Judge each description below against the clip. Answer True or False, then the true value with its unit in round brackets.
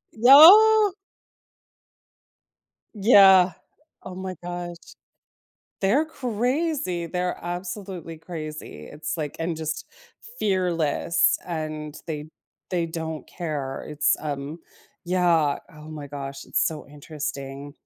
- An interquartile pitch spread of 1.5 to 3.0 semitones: False (3.8 semitones)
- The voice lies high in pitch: False (170 Hz)